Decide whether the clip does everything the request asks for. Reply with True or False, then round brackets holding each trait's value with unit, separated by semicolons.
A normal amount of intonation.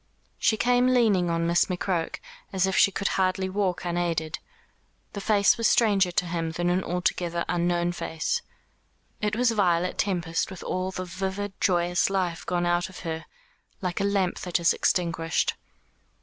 False (2.2 semitones)